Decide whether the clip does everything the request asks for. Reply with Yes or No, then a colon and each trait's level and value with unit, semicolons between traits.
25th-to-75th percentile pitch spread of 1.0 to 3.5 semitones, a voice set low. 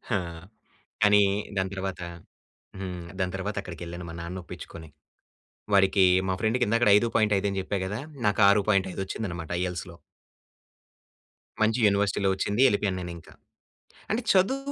Yes: narrow, 2.4 semitones; very low, 95 Hz